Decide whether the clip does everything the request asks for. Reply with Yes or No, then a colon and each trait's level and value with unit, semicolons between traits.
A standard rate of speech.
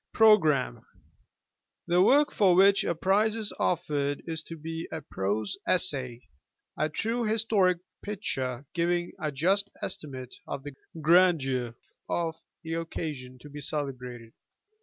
No: slow, 130 wpm